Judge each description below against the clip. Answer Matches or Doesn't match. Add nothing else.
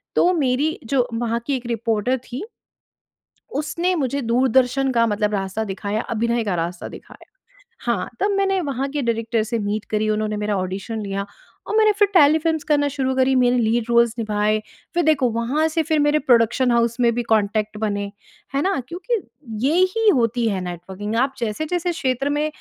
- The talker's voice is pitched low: Doesn't match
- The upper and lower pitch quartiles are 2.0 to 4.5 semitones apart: Doesn't match